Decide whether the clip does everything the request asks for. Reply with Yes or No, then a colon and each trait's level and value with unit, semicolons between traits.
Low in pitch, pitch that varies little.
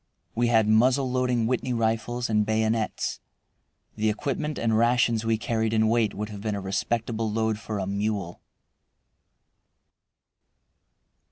Yes: low, 110 Hz; narrow, 1.7 semitones